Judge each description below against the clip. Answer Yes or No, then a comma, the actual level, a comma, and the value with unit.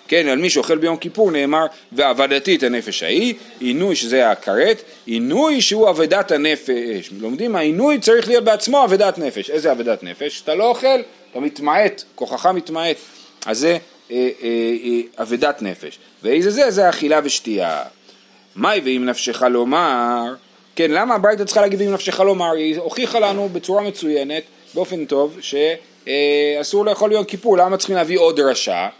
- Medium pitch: Yes, medium, 165 Hz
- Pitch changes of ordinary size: No, wide, 7.0 semitones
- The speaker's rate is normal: No, fast, 160 wpm